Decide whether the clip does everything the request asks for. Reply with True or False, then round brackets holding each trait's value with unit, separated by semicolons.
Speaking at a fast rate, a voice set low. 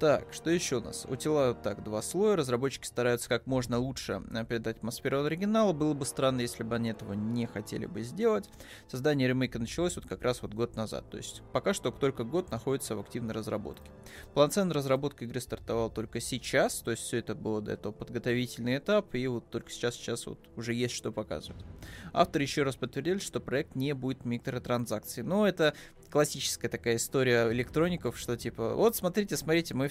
True (190 wpm; 120 Hz)